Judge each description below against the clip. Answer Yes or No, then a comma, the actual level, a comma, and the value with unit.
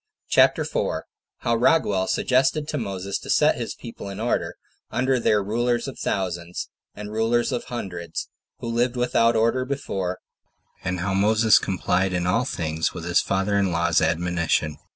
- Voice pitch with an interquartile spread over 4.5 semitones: Yes, average, 4.9 semitones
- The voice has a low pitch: Yes, low, 100 Hz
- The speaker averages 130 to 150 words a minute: No, average, 160 wpm